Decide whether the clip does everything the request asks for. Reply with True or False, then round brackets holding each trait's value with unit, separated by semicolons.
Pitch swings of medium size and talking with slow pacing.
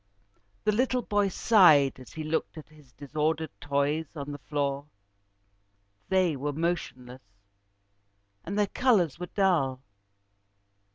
True (4.8 semitones; 120 wpm)